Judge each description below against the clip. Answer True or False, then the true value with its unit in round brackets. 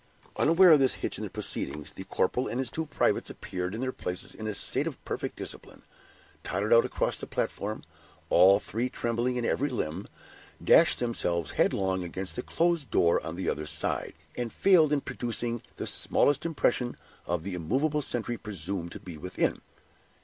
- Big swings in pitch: True (6.3 semitones)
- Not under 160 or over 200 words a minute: True (180 wpm)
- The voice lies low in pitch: True (115 Hz)